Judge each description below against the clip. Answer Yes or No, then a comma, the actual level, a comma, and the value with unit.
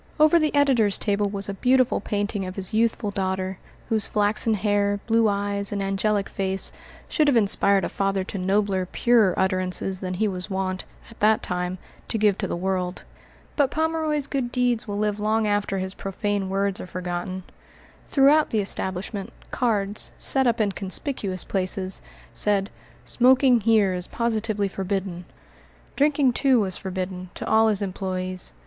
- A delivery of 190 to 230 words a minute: No, average, 160 wpm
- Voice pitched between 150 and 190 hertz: No, high, 200 Hz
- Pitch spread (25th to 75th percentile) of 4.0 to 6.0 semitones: No, average, 3.0 semitones